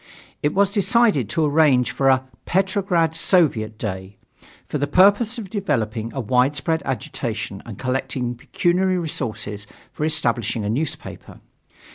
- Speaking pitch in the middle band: Yes, medium, 145 Hz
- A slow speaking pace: Yes, slow, 130 wpm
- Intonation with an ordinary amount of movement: No, wide, 7.1 semitones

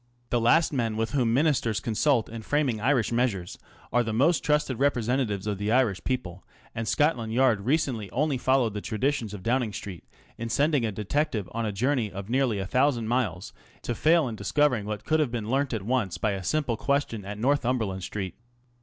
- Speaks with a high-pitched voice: No, low, 115 Hz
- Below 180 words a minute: No, average, 195 wpm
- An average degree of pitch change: Yes, average, 4.3 semitones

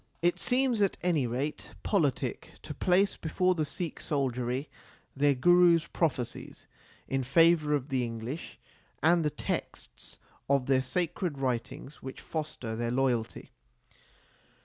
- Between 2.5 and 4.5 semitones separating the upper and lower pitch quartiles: No, average, 5.0 semitones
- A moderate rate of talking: No, slow, 130 wpm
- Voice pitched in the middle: Yes, medium, 145 Hz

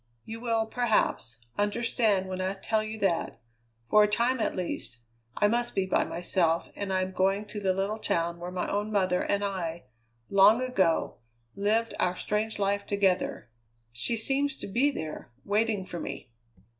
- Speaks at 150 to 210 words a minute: Yes, average, 170 wpm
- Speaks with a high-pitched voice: Yes, high, 200 Hz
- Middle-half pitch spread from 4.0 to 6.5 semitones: No, average, 3.0 semitones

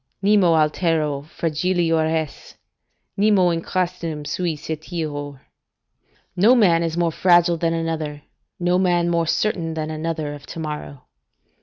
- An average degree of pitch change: No, narrow, 2.2 semitones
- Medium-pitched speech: Yes, medium, 165 Hz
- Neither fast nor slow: No, slow, 130 wpm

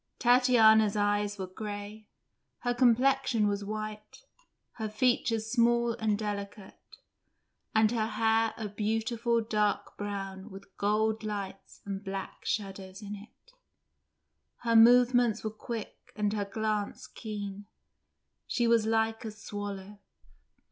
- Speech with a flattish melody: Yes, narrow, 1.8 semitones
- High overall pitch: Yes, high, 215 Hz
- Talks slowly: Yes, slow, 120 wpm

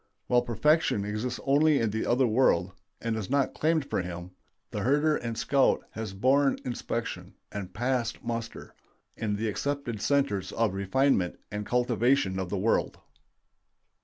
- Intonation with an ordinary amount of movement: Yes, average, 4.9 semitones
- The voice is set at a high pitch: No, low, 115 Hz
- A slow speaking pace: No, average, 150 wpm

